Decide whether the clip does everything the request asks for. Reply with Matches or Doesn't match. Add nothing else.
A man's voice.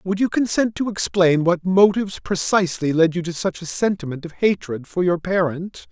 Matches